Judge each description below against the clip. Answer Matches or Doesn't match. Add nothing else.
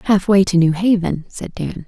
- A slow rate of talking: Matches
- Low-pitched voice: Doesn't match